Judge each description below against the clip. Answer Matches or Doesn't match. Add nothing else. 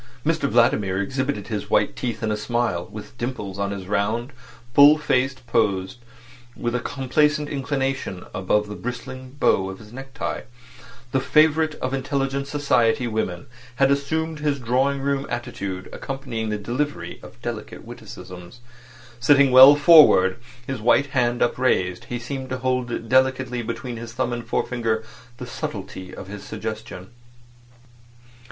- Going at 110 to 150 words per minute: Matches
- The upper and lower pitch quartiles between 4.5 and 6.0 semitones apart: Doesn't match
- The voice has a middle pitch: Doesn't match